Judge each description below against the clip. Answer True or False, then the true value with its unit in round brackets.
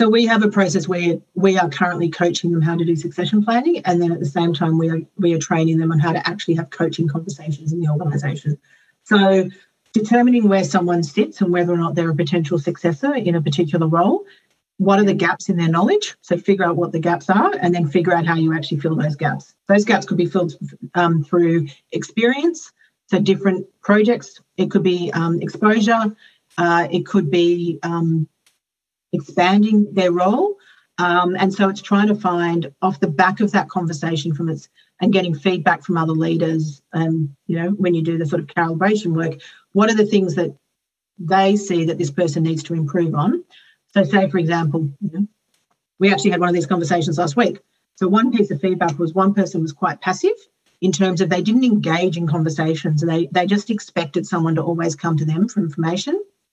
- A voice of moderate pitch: True (175 Hz)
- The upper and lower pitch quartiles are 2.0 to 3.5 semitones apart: True (2.6 semitones)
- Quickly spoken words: True (210 wpm)